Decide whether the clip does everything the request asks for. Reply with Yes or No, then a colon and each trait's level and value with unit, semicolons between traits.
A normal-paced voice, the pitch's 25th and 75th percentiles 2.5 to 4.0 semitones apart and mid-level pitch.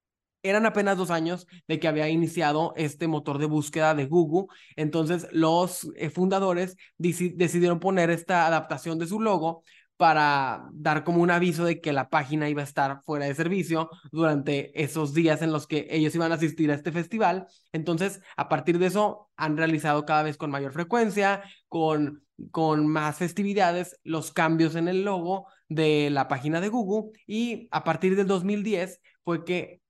Yes: average, 175 wpm; average, 2.8 semitones; medium, 165 Hz